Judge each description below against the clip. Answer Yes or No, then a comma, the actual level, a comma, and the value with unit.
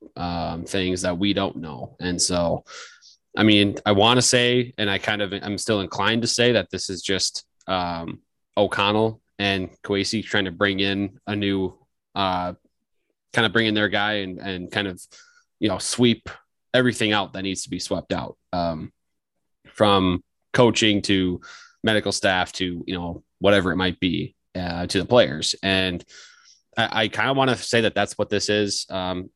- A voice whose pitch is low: Yes, low, 100 Hz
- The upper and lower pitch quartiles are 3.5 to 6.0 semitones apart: No, average, 2.8 semitones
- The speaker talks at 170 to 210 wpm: Yes, average, 185 wpm